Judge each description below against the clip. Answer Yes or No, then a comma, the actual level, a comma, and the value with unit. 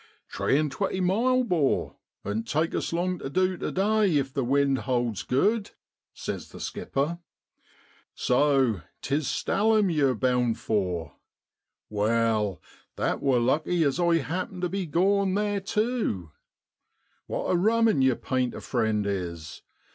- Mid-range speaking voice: Yes, medium, 145 Hz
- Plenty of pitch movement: Yes, wide, 7.5 semitones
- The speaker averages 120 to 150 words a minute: Yes, average, 145 wpm